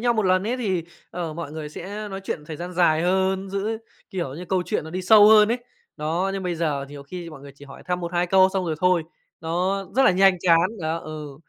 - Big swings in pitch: No, average, 3.3 semitones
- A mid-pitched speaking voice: Yes, medium, 180 Hz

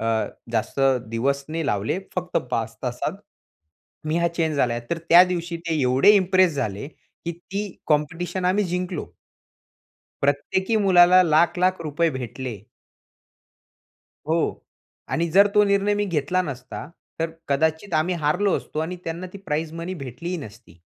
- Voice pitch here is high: No, medium, 165 Hz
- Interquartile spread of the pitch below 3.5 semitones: No, average, 4.6 semitones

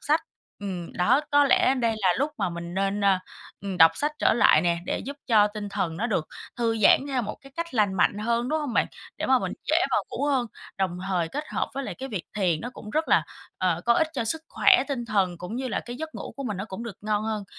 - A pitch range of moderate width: No, wide, 5.7 semitones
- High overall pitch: Yes, high, 220 Hz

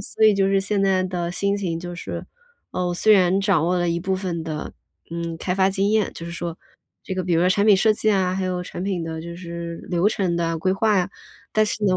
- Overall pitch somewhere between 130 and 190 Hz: Yes, medium, 185 Hz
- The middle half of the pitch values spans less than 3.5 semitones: Yes, narrow, 2.4 semitones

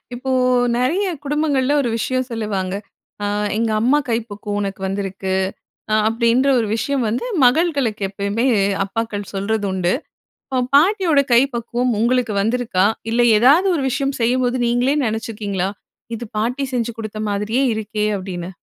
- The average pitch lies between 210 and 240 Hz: Yes, high, 230 Hz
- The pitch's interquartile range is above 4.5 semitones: No, average, 3.9 semitones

